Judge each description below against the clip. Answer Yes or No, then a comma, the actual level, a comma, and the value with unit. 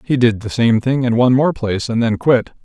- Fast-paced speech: Yes, fast, 275 wpm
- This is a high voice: No, low, 120 Hz